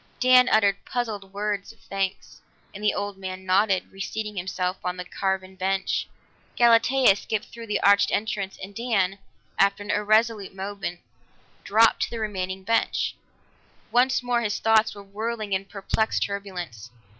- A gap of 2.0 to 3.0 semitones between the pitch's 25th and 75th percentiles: Yes, narrow, 2.4 semitones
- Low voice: No, high, 200 Hz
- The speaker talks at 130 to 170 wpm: Yes, average, 150 wpm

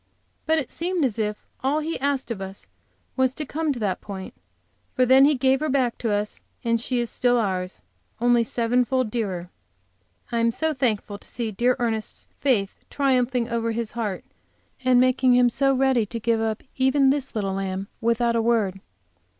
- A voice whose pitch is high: Yes, high, 240 Hz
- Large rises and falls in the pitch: No, average, 3.2 semitones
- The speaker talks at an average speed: Yes, average, 190 wpm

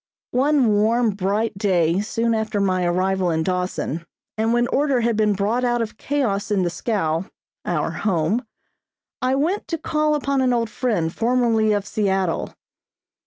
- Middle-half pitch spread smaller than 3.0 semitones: No, average, 4.3 semitones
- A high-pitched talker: Yes, high, 215 Hz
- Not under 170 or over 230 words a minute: No, average, 160 wpm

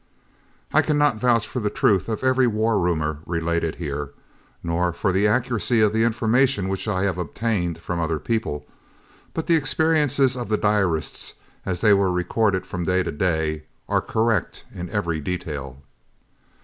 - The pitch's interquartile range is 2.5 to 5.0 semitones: No, wide, 5.4 semitones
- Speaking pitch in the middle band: No, low, 100 Hz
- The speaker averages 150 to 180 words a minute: Yes, average, 160 wpm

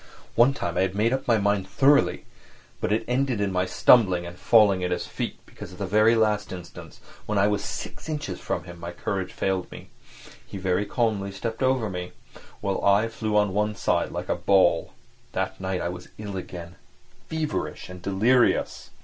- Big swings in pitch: No, average, 3.5 semitones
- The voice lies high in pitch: No, low, 100 Hz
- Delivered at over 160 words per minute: Yes, average, 190 wpm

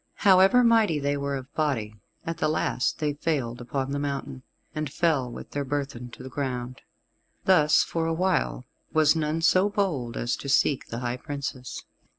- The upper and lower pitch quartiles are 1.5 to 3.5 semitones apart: No, average, 4.1 semitones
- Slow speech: No, average, 175 wpm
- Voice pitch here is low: No, medium, 145 Hz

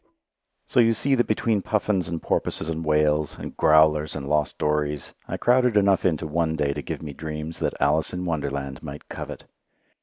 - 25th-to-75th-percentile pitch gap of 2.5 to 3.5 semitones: No, average, 4.0 semitones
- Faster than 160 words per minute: Yes, average, 185 wpm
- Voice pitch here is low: Yes, very low, 80 Hz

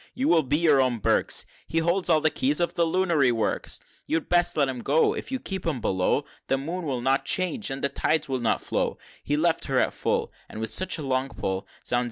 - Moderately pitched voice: Yes, medium, 145 Hz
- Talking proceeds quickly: Yes, fast, 245 wpm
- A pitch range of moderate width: Yes, average, 4.6 semitones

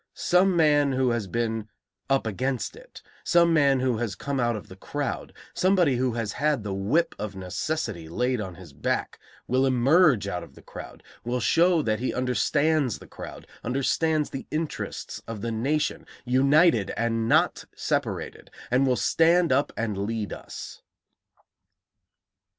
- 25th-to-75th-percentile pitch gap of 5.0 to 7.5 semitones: Yes, average, 5.3 semitones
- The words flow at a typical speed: Yes, average, 155 wpm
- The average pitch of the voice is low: Yes, low, 125 Hz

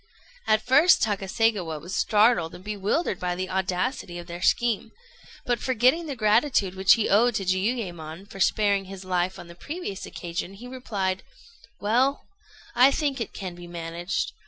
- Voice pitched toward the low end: No, high, 195 Hz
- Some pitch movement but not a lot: Yes, average, 4.8 semitones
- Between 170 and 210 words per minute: No, average, 160 wpm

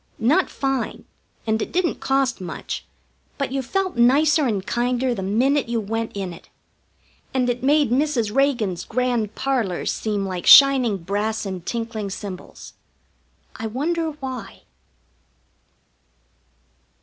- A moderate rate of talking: No, slow, 125 wpm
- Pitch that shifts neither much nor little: Yes, average, 4.6 semitones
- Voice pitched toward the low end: No, high, 240 Hz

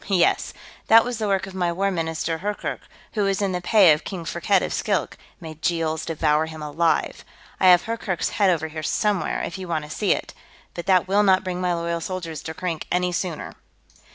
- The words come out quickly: Yes, fast, 210 wpm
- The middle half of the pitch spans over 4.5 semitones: No, average, 3.1 semitones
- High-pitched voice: No, medium, 180 Hz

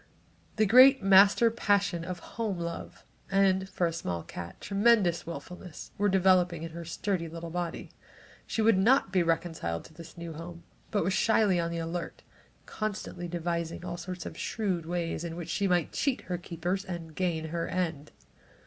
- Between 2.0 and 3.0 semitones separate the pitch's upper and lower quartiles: Yes, average, 2.7 semitones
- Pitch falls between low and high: Yes, medium, 175 Hz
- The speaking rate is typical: Yes, average, 175 wpm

